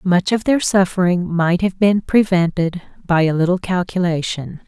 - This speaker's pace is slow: No, average, 155 wpm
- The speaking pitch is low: No, medium, 180 Hz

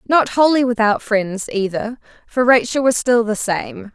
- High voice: Yes, high, 230 Hz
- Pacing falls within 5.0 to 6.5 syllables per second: No, 4.3 syllables/s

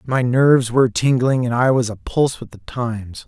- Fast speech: Yes, fast, 220 wpm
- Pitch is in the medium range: No, low, 125 Hz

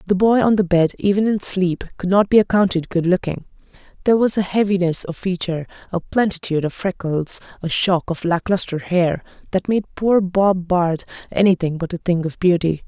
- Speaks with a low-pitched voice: No, medium, 185 Hz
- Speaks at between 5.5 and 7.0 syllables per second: No, 5.3 syllables/s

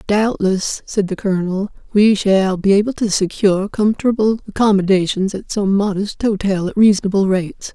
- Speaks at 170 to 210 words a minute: No, average, 145 wpm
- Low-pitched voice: No, high, 200 Hz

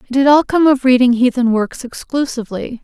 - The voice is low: No, very high, 255 Hz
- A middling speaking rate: Yes, average, 190 wpm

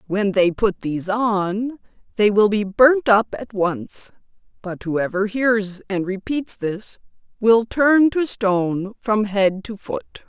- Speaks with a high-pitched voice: Yes, high, 210 Hz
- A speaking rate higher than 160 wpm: No, average, 150 wpm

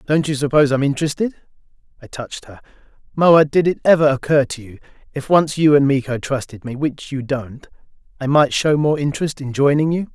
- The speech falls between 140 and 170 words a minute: No, average, 185 wpm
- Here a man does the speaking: Yes, male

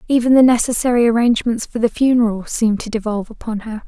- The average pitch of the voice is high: Yes, high, 230 Hz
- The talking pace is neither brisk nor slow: Yes, average, 185 wpm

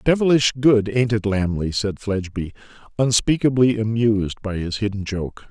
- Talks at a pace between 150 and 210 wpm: No, average, 140 wpm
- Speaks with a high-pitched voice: No, low, 110 Hz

